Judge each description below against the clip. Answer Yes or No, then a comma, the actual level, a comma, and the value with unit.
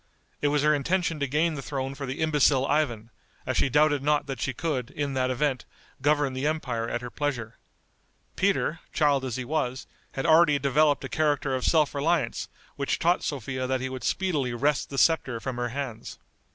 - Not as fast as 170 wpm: No, average, 195 wpm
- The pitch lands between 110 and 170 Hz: Yes, medium, 140 Hz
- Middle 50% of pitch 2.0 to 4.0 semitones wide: Yes, average, 2.7 semitones